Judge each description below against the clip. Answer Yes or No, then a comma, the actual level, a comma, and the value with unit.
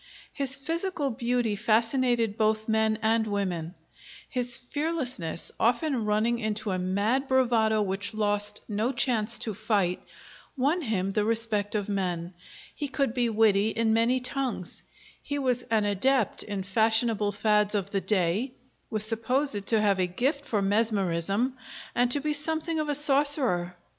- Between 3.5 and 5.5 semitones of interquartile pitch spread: Yes, average, 3.9 semitones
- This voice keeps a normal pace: Yes, average, 150 wpm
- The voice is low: No, high, 220 Hz